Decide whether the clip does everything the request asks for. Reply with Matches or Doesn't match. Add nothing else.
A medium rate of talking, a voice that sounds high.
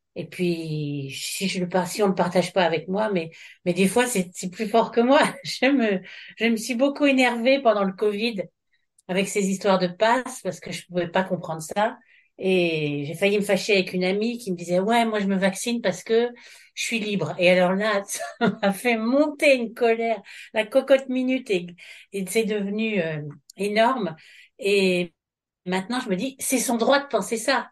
Matches